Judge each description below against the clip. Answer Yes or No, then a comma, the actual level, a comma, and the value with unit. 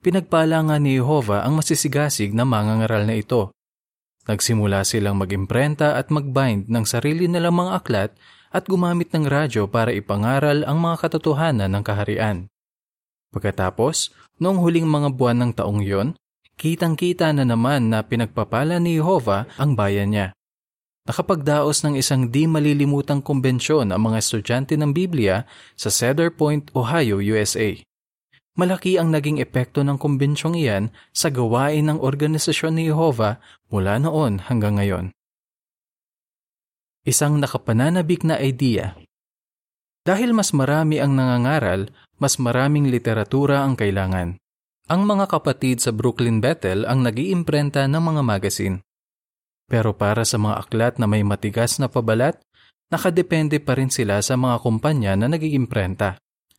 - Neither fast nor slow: Yes, average, 135 wpm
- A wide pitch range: Yes, wide, 6.0 semitones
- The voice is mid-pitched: No, low, 130 Hz